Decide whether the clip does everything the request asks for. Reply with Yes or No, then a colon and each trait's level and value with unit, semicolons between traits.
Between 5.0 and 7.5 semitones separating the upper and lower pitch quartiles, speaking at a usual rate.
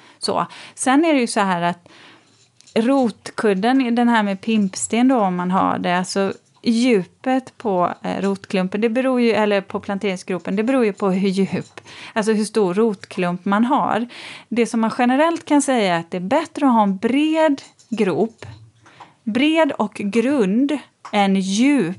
No: average, 4.5 semitones; average, 165 wpm